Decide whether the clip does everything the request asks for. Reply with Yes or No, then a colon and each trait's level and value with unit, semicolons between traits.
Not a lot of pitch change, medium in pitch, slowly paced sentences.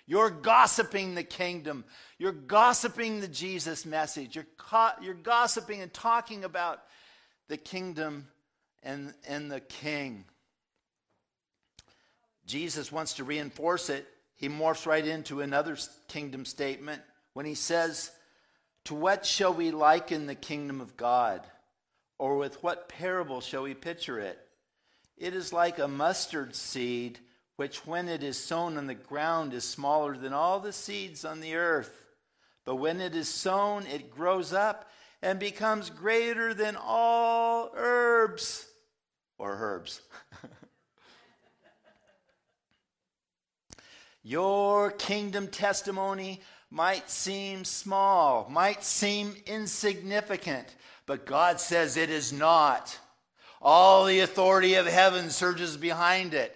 No: average, 5.2 semitones; medium, 175 Hz; slow, 125 wpm